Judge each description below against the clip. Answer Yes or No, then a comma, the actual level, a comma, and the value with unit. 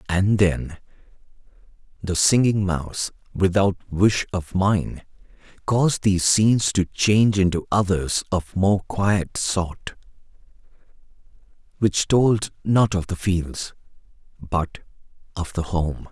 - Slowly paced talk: Yes, slow, 110 wpm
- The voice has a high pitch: No, very low, 95 Hz